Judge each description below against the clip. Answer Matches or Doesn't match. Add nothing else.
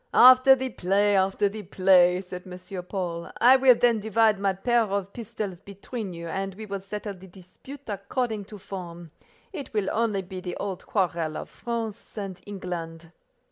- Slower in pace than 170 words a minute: Doesn't match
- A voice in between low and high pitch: Doesn't match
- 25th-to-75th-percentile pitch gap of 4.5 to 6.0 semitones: Doesn't match